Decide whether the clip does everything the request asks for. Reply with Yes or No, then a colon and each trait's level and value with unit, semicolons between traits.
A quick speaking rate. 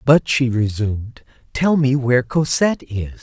No: average, 150 wpm